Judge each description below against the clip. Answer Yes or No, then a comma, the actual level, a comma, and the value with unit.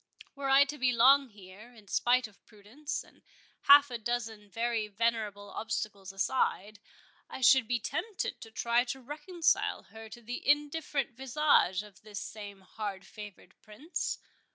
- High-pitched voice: Yes, high, 235 Hz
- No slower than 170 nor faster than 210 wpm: No, average, 155 wpm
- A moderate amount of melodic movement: Yes, average, 4.3 semitones